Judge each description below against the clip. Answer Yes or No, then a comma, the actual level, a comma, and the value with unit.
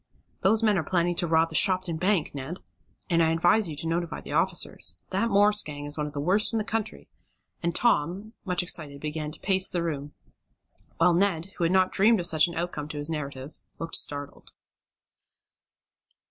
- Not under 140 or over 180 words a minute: No, average, 195 wpm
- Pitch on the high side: No, medium, 170 Hz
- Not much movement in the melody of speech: No, average, 3.9 semitones